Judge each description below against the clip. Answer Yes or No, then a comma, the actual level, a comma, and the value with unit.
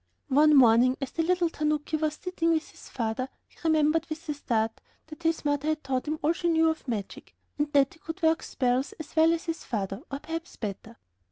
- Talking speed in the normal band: No, fast, 215 wpm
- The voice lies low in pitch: No, very high, 305 Hz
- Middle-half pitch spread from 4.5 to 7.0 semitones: No, average, 3.9 semitones